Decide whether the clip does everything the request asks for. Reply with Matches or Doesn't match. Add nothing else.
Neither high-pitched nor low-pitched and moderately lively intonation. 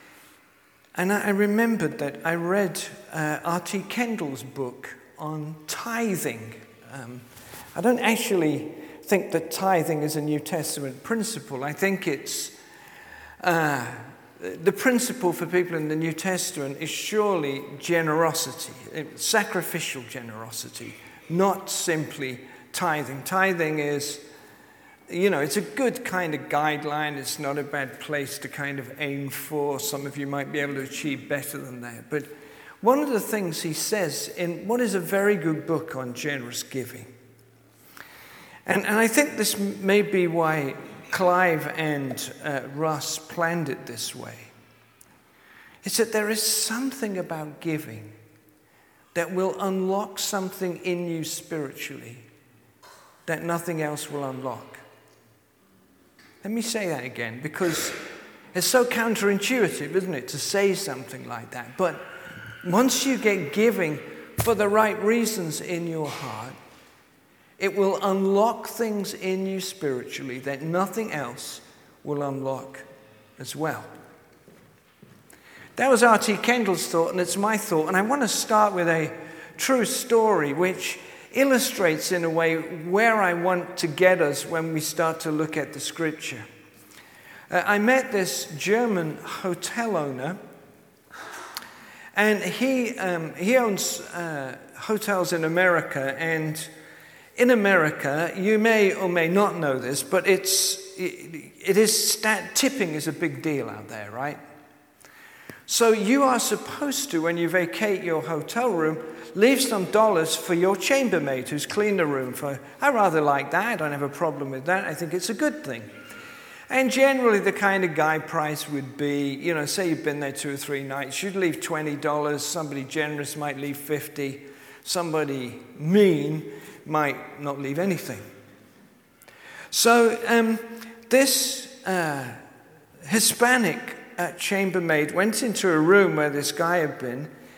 Doesn't match